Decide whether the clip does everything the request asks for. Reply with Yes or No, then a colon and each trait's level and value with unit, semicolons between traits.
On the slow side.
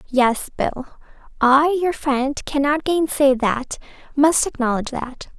Yes: slow, 120 wpm